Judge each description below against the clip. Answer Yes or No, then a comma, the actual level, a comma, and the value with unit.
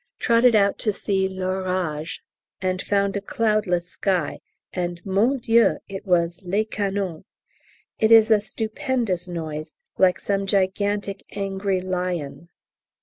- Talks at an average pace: No, slow, 125 wpm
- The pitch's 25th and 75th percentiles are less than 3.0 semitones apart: Yes, narrow, 2.4 semitones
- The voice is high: Yes, high, 195 Hz